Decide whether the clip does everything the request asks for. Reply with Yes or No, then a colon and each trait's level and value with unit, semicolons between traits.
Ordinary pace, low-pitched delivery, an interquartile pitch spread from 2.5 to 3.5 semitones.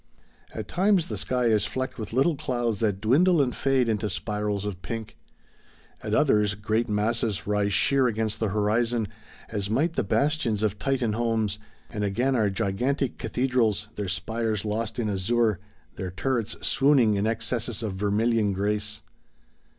Yes: average, 155 wpm; low, 110 Hz; average, 2.9 semitones